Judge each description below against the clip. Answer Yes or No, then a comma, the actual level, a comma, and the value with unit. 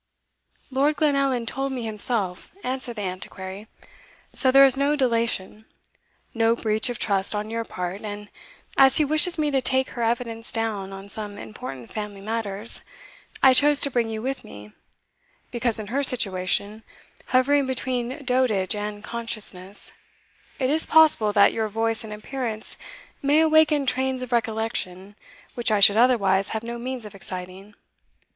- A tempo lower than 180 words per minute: Yes, average, 155 wpm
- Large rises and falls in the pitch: No, average, 4.0 semitones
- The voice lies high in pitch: Yes, high, 230 Hz